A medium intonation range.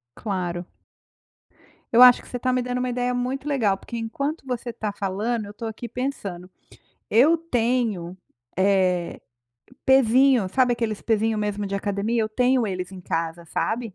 Yes: average, 4.0 semitones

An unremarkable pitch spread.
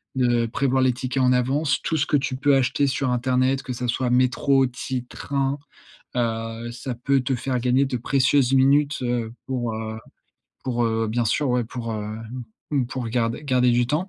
No: narrow, 2.1 semitones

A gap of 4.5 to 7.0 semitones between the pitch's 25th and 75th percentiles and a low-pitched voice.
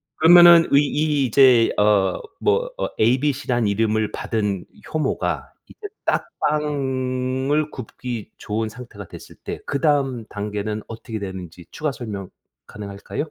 Yes: wide, 5.5 semitones; low, 125 Hz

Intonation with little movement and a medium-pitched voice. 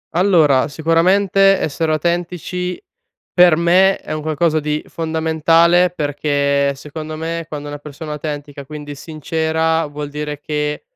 Yes: narrow, 2.2 semitones; medium, 155 Hz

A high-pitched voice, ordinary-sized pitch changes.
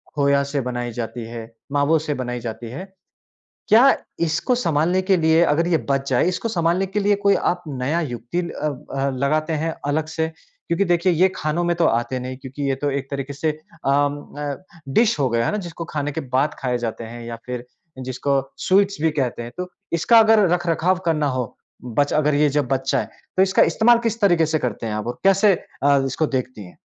No: medium, 150 Hz; average, 4.9 semitones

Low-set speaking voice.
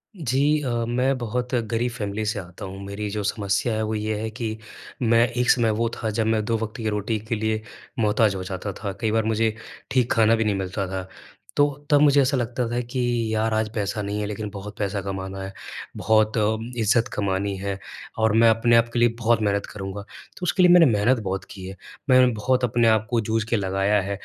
Yes: low, 110 Hz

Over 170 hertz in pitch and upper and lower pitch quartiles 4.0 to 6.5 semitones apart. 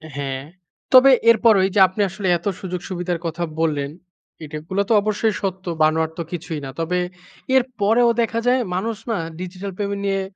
Yes: high, 190 Hz; average, 4.5 semitones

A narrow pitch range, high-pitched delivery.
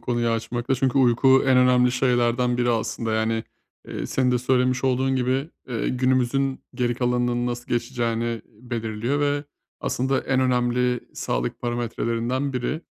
No: narrow, 1.6 semitones; low, 125 Hz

